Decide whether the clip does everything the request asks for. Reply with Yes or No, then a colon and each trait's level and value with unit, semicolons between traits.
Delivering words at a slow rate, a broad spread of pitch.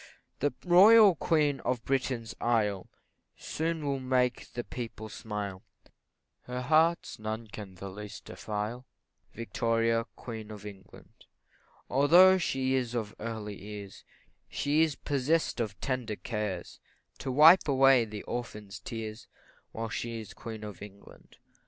No: slow, 130 wpm; average, 4.3 semitones